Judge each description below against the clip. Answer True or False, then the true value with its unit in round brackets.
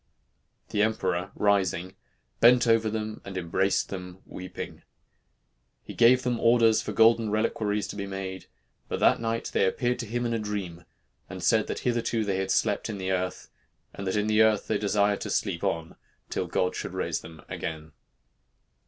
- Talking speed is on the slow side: False (180 wpm)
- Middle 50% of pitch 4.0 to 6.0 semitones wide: False (3.2 semitones)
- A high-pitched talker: False (105 Hz)